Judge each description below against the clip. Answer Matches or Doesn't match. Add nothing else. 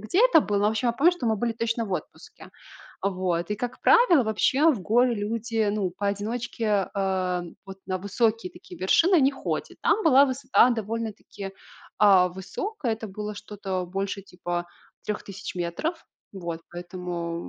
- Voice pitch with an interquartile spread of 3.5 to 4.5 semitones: Matches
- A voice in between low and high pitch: Doesn't match